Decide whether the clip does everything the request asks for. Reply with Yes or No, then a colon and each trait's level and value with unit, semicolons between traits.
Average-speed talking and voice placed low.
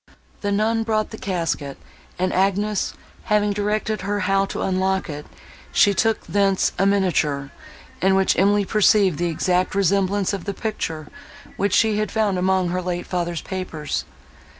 No: average, 155 wpm; high, 195 Hz